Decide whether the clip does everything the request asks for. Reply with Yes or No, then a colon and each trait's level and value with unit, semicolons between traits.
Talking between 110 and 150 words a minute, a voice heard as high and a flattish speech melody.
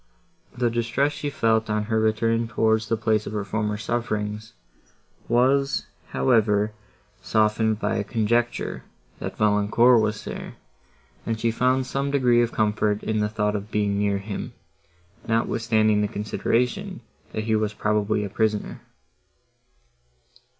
No: slow, 135 wpm; low, 110 Hz; narrow, 1.9 semitones